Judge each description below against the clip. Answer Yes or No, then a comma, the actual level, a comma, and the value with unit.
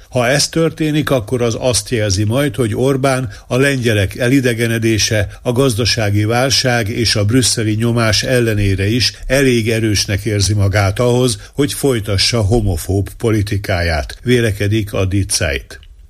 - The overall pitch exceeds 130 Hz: No, low, 115 Hz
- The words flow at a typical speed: Yes, average, 125 wpm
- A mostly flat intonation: No, average, 3.6 semitones